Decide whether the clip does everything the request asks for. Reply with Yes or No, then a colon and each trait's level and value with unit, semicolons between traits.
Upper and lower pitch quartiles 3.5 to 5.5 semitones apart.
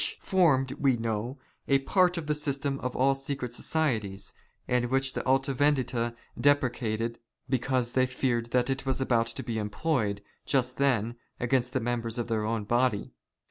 No: average, 2.7 semitones